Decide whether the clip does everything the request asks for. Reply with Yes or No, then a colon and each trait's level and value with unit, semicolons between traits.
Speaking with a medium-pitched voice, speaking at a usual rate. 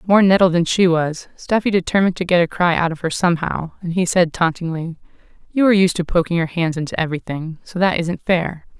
No: medium, 175 Hz; fast, 225 wpm